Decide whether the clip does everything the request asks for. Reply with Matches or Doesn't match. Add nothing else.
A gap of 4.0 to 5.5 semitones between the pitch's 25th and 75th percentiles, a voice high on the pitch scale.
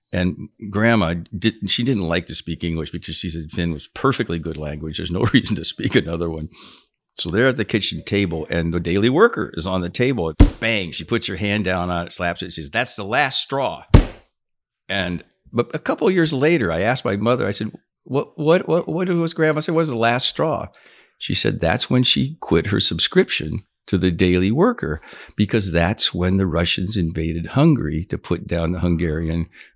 Doesn't match